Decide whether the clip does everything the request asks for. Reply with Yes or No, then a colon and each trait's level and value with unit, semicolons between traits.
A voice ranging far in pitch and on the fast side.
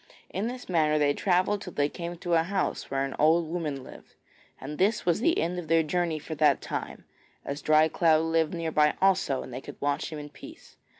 No: average, 2.9 semitones; fast, 225 wpm